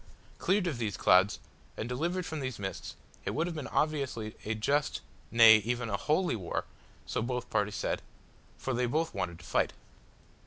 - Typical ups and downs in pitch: No, wide, 6.1 semitones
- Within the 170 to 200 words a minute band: Yes, average, 180 wpm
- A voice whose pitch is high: No, low, 120 Hz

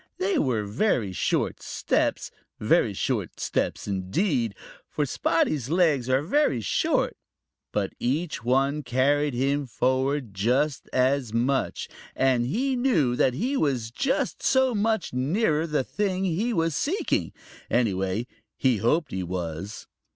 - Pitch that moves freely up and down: Yes, wide, 6.2 semitones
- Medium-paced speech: No, slow, 130 wpm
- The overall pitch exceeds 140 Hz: No, low, 135 Hz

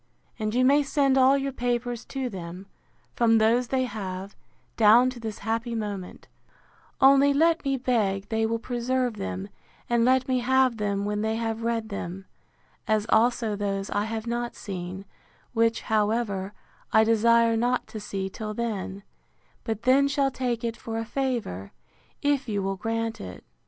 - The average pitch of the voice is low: No, high, 225 Hz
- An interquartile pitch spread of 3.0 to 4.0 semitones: Yes, average, 3.3 semitones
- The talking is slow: No, average, 165 wpm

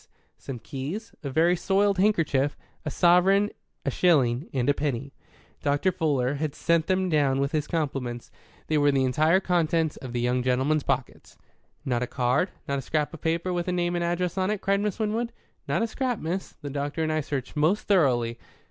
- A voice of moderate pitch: Yes, medium, 155 Hz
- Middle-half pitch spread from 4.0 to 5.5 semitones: Yes, average, 4.9 semitones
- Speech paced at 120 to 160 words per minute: No, average, 195 wpm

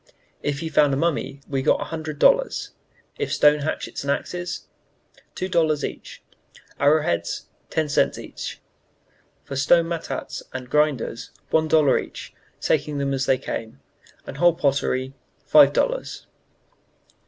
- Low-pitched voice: No, medium, 150 Hz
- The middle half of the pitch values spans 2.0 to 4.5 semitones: Yes, average, 3.0 semitones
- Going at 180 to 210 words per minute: No, average, 140 wpm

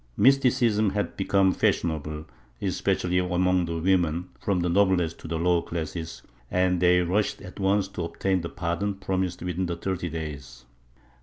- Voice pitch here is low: Yes, very low, 90 Hz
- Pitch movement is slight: Yes, narrow, 2.3 semitones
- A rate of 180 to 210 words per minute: No, average, 155 wpm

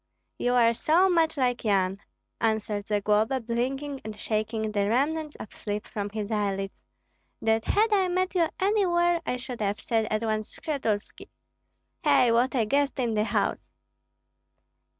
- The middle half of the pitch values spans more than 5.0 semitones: Yes, wide, 5.4 semitones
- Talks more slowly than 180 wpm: Yes, average, 150 wpm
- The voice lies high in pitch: Yes, high, 230 Hz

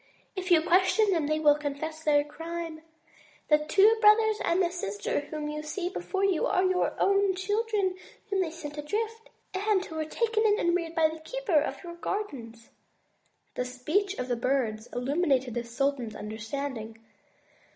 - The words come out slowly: No, average, 170 wpm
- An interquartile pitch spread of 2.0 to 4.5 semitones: No, average, 5.3 semitones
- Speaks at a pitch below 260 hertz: No, very high, 320 Hz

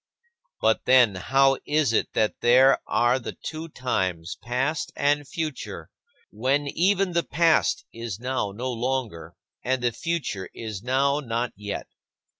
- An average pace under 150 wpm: Yes, average, 140 wpm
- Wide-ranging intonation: No, average, 4.2 semitones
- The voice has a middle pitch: No, low, 130 Hz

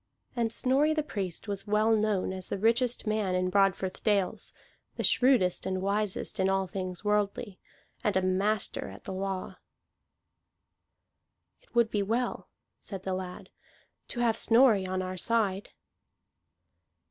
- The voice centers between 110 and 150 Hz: No, high, 200 Hz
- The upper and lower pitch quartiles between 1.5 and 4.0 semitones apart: Yes, average, 3.0 semitones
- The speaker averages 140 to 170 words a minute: Yes, average, 145 wpm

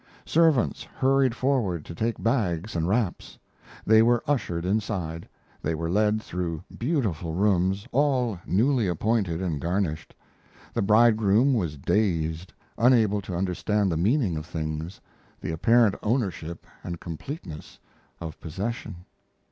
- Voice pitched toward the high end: No, low, 100 Hz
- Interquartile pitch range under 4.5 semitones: No, wide, 5.5 semitones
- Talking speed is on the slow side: Yes, slow, 125 wpm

